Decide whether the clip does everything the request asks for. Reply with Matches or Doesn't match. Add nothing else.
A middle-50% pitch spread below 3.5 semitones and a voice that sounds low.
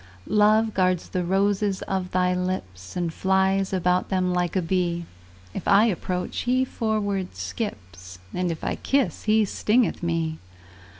Doesn't match